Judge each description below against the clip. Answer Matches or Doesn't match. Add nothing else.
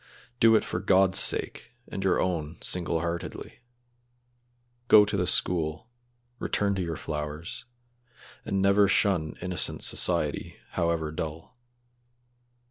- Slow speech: Matches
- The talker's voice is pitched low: Matches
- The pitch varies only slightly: Doesn't match